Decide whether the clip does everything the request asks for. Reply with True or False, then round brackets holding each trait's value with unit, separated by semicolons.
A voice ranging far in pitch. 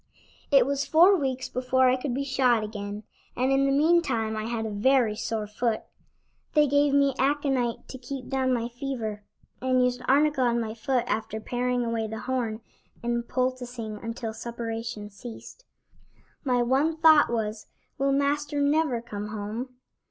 False (3.4 semitones)